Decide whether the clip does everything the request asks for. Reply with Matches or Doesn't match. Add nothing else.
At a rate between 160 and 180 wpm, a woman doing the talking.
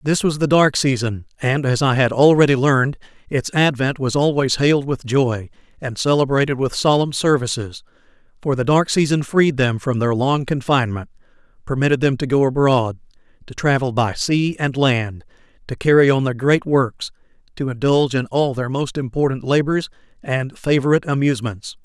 Doesn't match